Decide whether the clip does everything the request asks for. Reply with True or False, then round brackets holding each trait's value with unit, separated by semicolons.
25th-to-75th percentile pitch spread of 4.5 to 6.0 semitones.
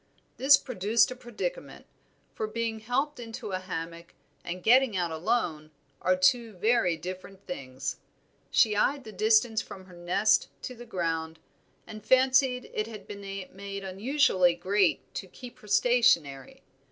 True (4.9 semitones)